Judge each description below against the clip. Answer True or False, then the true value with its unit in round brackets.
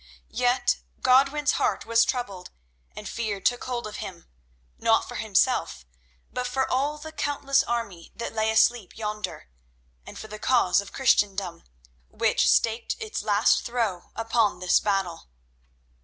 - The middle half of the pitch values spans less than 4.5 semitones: True (3.9 semitones)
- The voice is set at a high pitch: True (225 Hz)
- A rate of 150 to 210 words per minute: False (140 wpm)